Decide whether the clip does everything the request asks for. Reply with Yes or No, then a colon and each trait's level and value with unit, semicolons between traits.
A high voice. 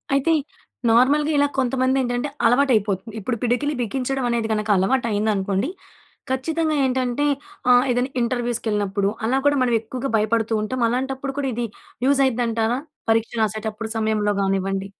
Yes: high, 240 Hz